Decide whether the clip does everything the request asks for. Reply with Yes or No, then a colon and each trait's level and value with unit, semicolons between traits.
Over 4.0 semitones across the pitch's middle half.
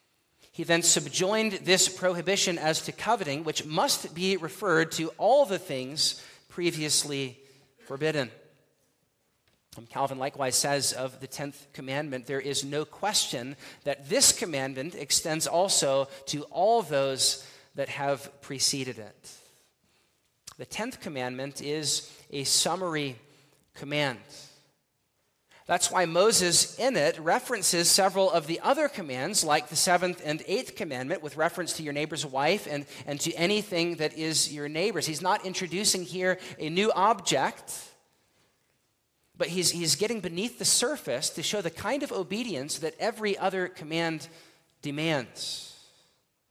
Yes: average, 4.6 semitones